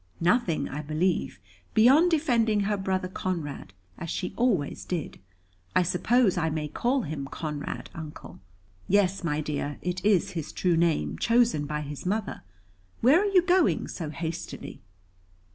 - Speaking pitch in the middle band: Yes, medium, 180 Hz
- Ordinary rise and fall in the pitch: No, wide, 6.6 semitones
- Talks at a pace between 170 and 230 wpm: No, average, 145 wpm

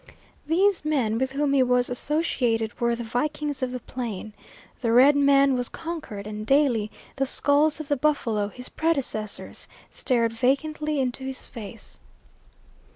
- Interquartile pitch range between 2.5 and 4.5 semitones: Yes, average, 4.1 semitones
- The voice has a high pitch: Yes, very high, 260 Hz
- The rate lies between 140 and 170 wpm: Yes, average, 150 wpm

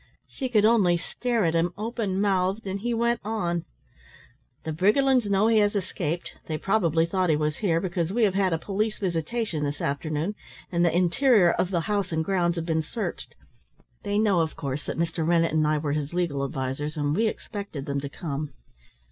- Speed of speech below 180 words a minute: No, average, 200 wpm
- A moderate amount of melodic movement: Yes, average, 4.6 semitones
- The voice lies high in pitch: No, medium, 175 Hz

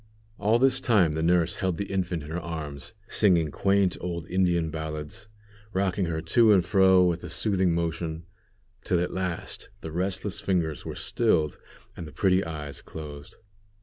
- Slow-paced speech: No, average, 165 wpm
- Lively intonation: No, average, 3.0 semitones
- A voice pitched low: Yes, very low, 85 Hz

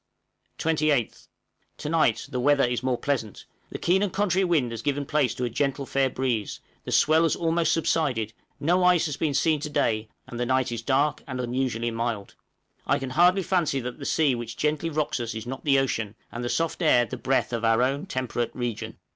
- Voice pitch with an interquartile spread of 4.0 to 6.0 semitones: Yes, average, 4.3 semitones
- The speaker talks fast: Yes, fast, 210 wpm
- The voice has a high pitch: No, low, 135 Hz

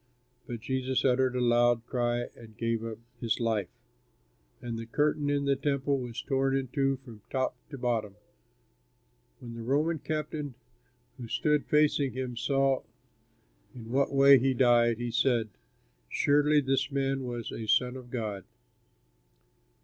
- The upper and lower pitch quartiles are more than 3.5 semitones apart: No, average, 2.7 semitones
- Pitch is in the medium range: No, low, 130 Hz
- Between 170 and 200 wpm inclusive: No, average, 155 wpm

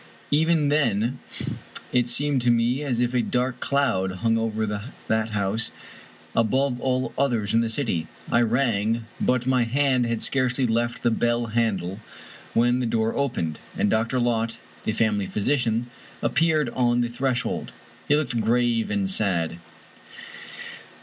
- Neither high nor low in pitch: No, low, 120 Hz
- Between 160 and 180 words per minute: No, average, 145 wpm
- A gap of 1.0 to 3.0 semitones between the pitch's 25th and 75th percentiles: Yes, narrow, 2.5 semitones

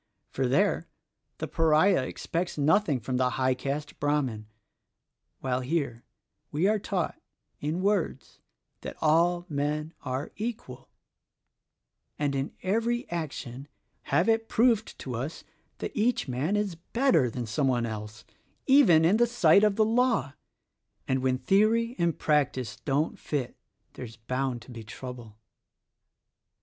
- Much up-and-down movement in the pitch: Yes, wide, 7.5 semitones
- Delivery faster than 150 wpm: No, average, 140 wpm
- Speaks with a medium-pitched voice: Yes, medium, 150 Hz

